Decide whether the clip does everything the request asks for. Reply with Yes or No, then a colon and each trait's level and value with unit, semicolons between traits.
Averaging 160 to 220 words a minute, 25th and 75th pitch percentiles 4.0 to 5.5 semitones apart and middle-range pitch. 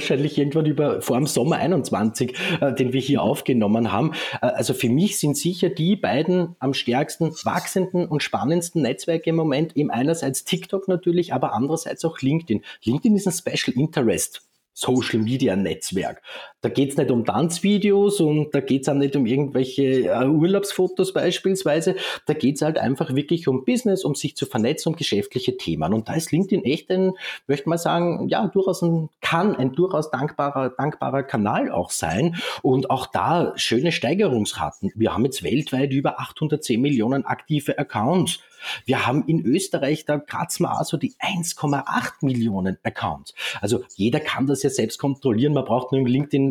Yes: average, 170 wpm; average, 4.4 semitones; medium, 150 Hz